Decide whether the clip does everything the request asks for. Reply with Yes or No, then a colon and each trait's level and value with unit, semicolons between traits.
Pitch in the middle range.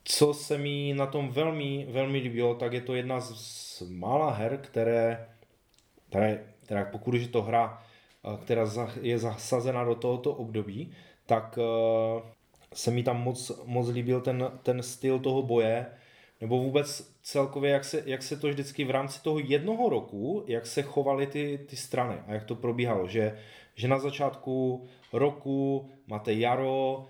No: low, 125 Hz